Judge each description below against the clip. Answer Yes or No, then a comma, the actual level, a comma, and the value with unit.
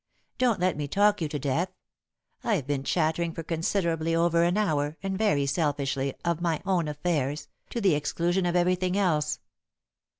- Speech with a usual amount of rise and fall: Yes, average, 3.6 semitones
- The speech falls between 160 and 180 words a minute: Yes, average, 165 wpm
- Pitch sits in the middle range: Yes, medium, 170 Hz